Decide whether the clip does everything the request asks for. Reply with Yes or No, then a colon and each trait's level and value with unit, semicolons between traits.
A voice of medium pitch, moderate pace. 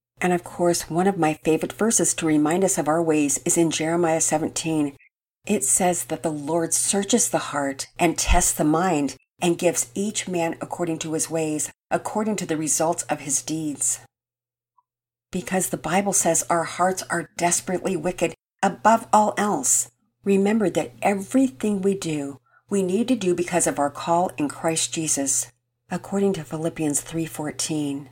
Yes: medium, 165 Hz; average, 165 wpm